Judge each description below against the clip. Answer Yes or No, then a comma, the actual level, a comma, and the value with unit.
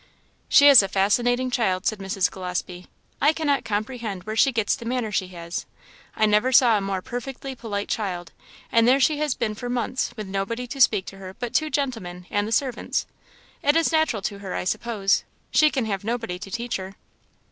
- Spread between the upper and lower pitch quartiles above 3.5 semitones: Yes, average, 4.5 semitones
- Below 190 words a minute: No, average, 200 wpm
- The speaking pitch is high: Yes, high, 220 Hz